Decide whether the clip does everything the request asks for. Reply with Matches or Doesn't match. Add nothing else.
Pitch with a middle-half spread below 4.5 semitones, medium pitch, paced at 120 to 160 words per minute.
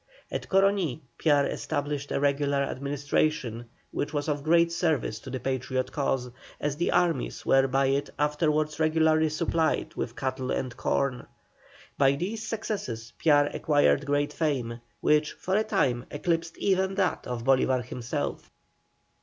Matches